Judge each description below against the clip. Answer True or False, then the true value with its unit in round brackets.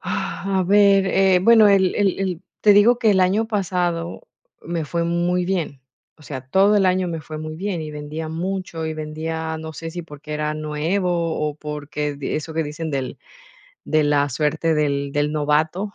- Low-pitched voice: False (165 Hz)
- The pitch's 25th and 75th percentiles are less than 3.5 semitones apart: False (3.9 semitones)